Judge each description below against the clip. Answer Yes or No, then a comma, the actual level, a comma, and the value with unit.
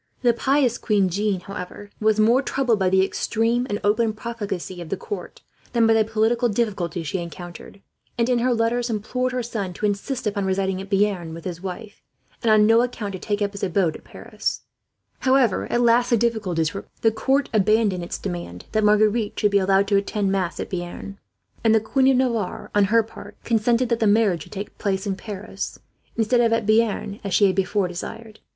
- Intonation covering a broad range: No, average, 3.1 semitones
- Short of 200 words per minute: No, fast, 205 wpm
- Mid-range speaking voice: No, high, 210 Hz